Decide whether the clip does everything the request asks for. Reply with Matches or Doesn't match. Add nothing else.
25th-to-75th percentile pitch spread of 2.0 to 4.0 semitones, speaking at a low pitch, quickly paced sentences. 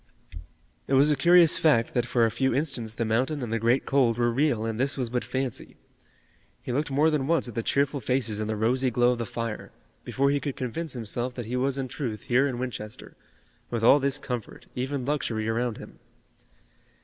Matches